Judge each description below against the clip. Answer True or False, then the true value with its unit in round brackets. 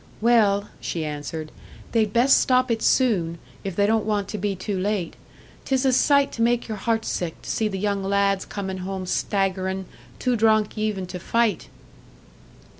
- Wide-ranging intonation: False (3.1 semitones)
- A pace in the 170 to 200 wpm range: True (175 wpm)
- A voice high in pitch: True (205 Hz)